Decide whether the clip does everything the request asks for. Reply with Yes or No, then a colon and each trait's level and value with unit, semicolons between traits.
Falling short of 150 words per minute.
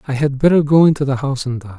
No: fast, 305 wpm